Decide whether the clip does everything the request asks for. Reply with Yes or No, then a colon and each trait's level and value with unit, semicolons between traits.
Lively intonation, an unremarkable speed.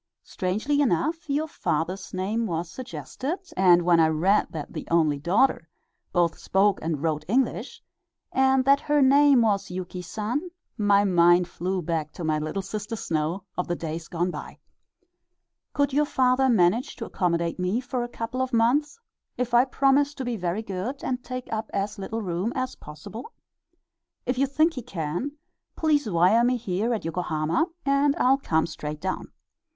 Yes: wide, 6.9 semitones; average, 170 wpm